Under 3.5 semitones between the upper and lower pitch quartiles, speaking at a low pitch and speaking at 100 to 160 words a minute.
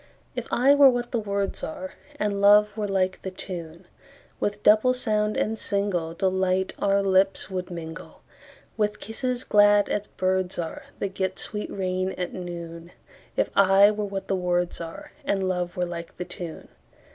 No: narrow, 2.6 semitones; high, 195 Hz; average, 145 wpm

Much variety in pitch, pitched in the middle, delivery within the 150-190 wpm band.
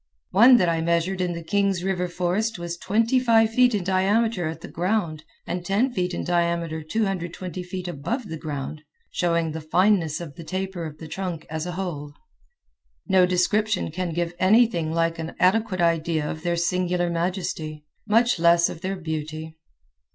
No: average, 2.8 semitones; medium, 175 Hz; average, 175 wpm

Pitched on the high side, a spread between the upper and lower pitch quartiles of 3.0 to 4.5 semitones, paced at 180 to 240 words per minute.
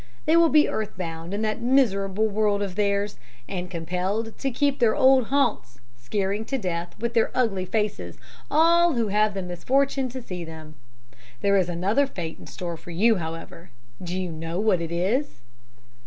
No: high, 200 Hz; average, 5.0 semitones; average, 185 wpm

